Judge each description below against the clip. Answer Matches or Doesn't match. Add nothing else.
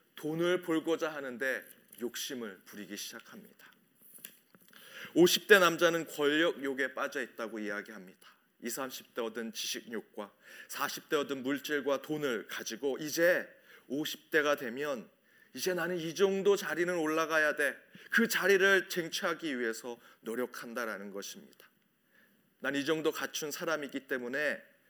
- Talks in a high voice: Doesn't match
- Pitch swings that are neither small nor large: Matches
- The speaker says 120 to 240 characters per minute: Doesn't match